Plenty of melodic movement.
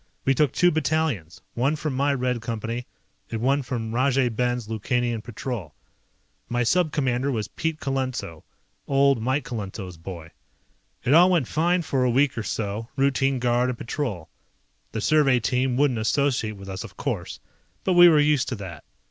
No: average, 3.8 semitones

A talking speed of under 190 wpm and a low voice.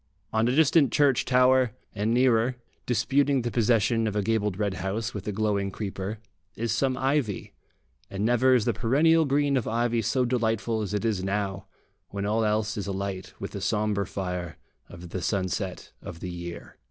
Yes: average, 180 wpm; low, 110 Hz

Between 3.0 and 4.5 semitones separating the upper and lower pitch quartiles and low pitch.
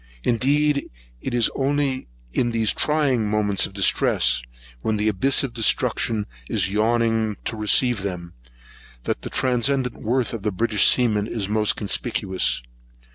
Yes: average, 3.4 semitones; low, 115 Hz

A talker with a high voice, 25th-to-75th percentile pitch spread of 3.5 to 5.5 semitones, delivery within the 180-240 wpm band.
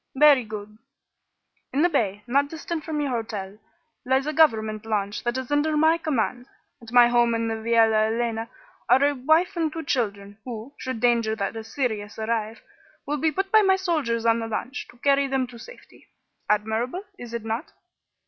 Yes: high, 240 Hz; average, 4.7 semitones; average, 185 wpm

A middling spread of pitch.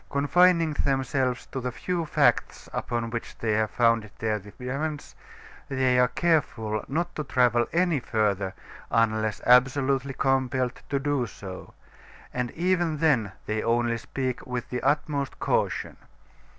Yes: average, 3.8 semitones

